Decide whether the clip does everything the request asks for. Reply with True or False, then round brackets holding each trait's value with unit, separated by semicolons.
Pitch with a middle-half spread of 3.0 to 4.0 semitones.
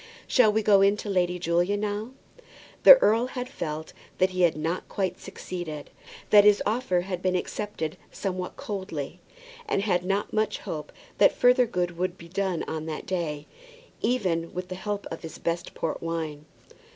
True (3.6 semitones)